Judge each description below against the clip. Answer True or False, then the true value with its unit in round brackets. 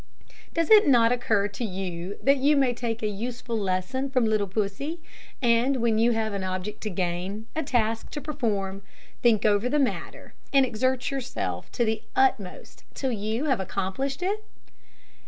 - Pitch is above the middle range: True (230 Hz)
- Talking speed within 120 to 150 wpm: False (170 wpm)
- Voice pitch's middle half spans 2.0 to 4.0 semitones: False (4.7 semitones)